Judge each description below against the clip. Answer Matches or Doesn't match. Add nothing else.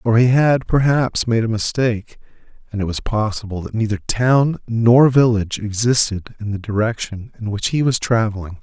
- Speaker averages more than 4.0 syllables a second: Matches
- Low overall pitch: Matches